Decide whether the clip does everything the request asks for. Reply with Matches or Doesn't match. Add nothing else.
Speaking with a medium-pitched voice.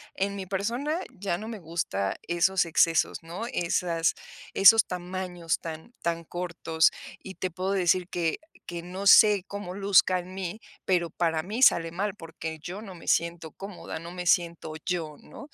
Matches